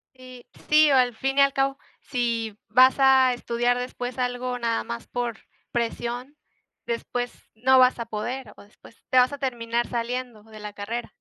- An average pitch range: No, narrow, 1.8 semitones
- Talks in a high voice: Yes, high, 245 Hz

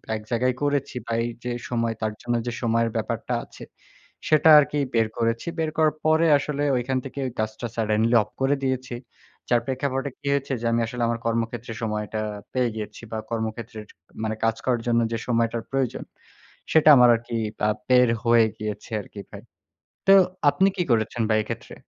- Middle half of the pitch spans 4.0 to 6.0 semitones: No, average, 2.8 semitones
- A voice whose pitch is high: No, low, 120 Hz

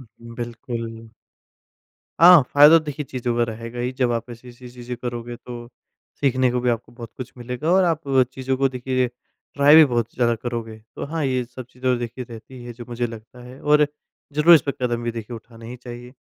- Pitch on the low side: Yes, low, 125 Hz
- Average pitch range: No, narrow, 1.8 semitones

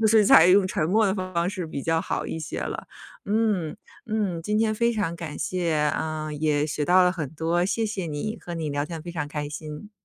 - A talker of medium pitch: Yes, medium, 170 Hz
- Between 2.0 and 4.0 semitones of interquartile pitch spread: No, average, 4.7 semitones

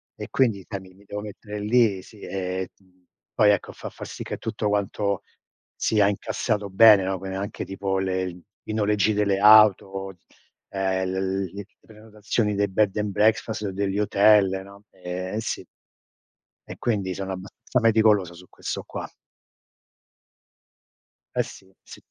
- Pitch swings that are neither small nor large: No, narrow, 1.8 semitones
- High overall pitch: No, low, 100 Hz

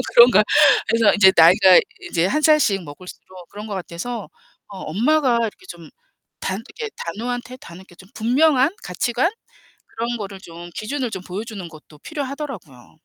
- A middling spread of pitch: No, wide, 5.7 semitones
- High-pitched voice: Yes, high, 215 Hz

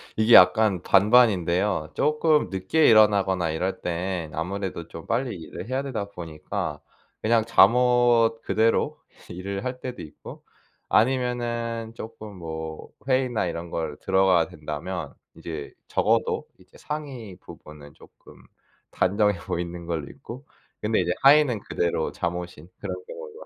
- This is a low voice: Yes, low, 100 Hz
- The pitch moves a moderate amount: No, wide, 5.7 semitones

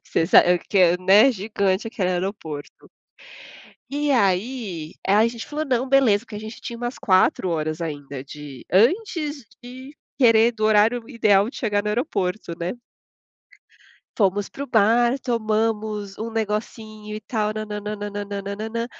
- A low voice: No, high, 215 Hz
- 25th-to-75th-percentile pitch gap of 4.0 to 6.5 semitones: No, average, 3.3 semitones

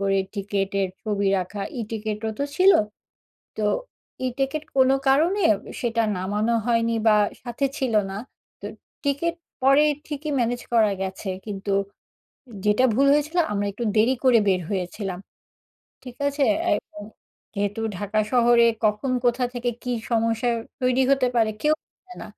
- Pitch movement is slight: No, average, 4.2 semitones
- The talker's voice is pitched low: No, high, 230 Hz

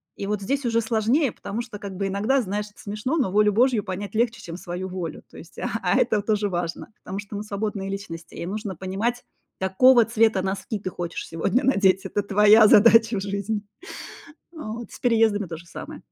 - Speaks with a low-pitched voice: No, high, 210 Hz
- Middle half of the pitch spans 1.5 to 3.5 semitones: Yes, average, 2.9 semitones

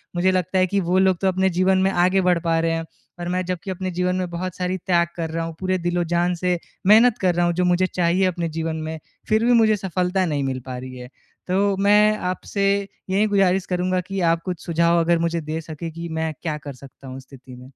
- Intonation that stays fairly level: Yes, narrow, 2.2 semitones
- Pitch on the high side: No, medium, 180 Hz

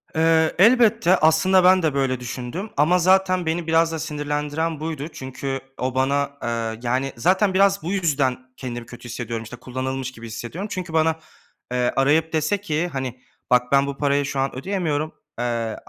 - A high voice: No, medium, 145 Hz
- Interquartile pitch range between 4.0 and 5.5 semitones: Yes, average, 4.5 semitones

